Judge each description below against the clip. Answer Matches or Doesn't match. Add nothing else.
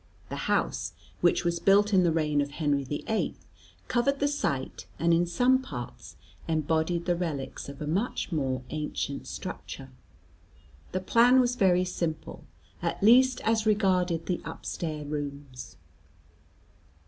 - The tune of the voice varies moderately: Doesn't match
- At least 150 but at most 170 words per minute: Doesn't match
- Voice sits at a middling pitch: Matches